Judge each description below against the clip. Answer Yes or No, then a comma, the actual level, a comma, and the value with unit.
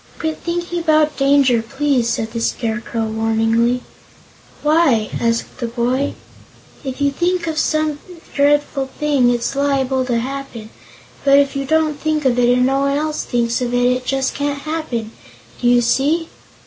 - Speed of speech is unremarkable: Yes, average, 160 wpm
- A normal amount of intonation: Yes, average, 3.7 semitones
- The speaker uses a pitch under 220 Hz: No, very high, 270 Hz